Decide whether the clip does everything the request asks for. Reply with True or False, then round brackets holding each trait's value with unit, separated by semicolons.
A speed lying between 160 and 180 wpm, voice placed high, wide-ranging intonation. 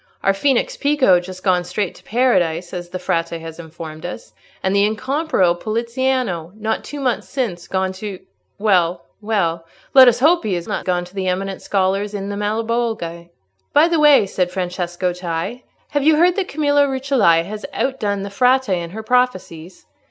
True (175 wpm; 200 Hz; 6.0 semitones)